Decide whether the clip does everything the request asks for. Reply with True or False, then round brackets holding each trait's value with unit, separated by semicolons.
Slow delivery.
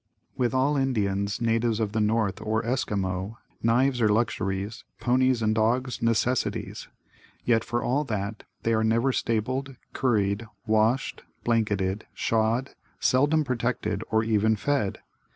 True (130 wpm)